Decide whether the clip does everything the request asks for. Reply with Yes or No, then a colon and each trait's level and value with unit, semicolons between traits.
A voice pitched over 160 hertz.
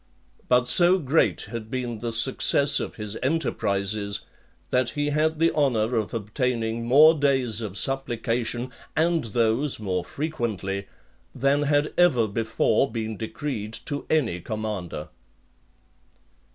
No: low, 120 Hz